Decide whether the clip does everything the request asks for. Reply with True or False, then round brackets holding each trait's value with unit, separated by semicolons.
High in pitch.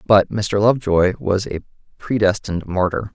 False (100 Hz)